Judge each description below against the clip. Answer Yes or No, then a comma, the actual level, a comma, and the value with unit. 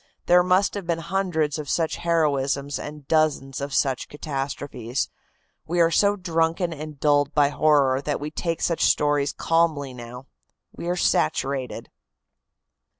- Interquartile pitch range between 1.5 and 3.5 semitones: Yes, average, 3.1 semitones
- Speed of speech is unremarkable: Yes, average, 145 wpm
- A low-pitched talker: No, medium, 150 Hz